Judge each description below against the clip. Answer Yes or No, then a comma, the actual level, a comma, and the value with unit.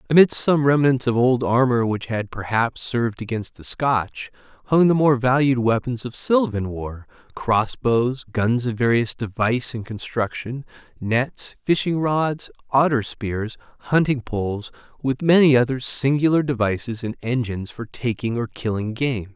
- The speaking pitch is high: No, low, 125 Hz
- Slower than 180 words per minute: Yes, average, 150 wpm